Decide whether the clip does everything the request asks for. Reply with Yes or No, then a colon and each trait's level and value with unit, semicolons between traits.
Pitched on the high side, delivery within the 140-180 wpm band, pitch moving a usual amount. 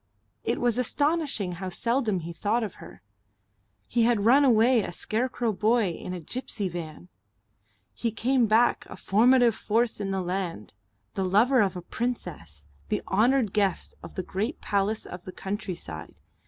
Yes: high, 215 Hz; average, 160 wpm; average, 4.5 semitones